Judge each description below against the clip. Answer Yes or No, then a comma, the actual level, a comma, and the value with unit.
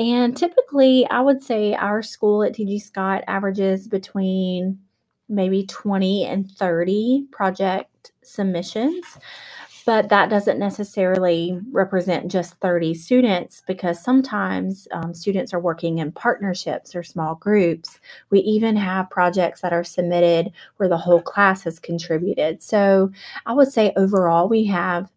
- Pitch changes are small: No, average, 3.2 semitones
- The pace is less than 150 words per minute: Yes, slow, 135 wpm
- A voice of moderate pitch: No, high, 195 Hz